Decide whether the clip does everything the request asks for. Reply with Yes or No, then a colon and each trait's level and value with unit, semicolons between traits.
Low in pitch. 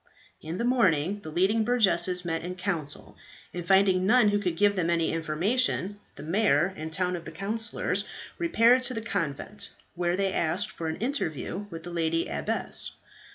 No: medium, 185 Hz